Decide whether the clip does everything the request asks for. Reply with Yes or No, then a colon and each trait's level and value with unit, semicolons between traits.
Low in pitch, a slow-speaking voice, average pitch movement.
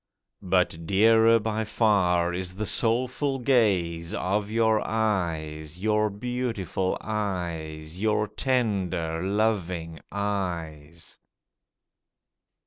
Yes: low, 100 Hz; slow, 85 wpm; average, 4.4 semitones